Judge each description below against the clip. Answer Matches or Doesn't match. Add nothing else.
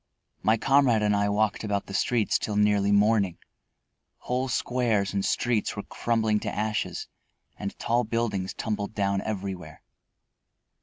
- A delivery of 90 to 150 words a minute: Matches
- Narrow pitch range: Matches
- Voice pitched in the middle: Doesn't match